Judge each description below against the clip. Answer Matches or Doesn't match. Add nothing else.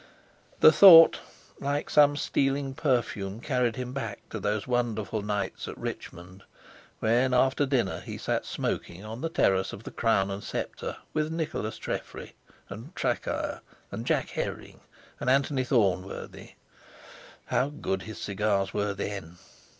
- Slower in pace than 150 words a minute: Matches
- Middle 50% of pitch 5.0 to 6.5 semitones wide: Matches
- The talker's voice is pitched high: Doesn't match